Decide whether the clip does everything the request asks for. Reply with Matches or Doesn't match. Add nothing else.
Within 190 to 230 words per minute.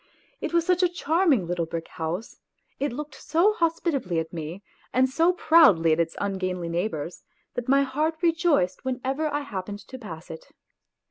Doesn't match